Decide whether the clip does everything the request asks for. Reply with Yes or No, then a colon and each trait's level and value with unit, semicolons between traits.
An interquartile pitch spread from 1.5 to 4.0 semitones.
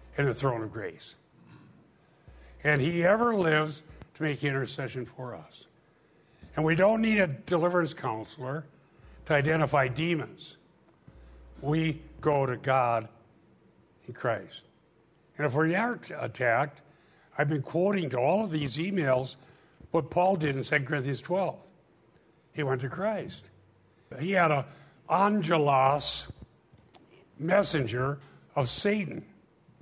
No: average, 4.4 semitones